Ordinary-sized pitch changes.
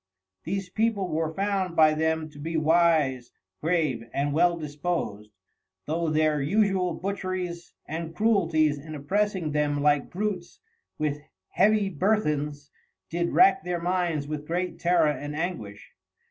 Yes: average, 3.6 semitones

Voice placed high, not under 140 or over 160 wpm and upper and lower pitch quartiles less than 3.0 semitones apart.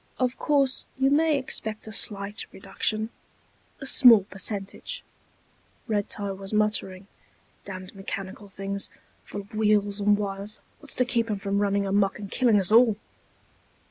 Yes: high, 205 Hz; average, 145 wpm; narrow, 2.5 semitones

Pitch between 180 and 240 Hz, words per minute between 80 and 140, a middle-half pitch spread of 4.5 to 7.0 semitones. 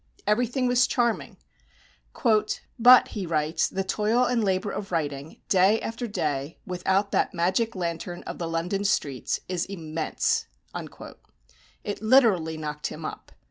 Yes: high, 190 Hz; slow, 135 wpm; average, 5.0 semitones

